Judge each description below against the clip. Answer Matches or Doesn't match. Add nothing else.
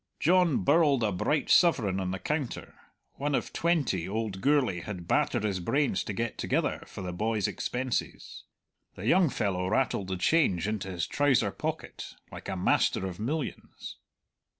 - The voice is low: Matches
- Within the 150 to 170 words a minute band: Matches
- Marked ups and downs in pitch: Matches